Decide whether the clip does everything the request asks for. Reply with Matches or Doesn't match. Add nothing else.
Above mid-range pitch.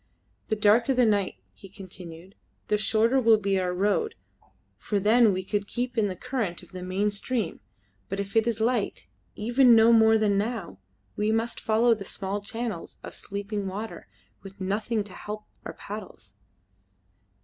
Matches